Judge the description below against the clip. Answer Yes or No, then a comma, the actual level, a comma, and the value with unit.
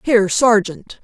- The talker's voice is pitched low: No, high, 215 Hz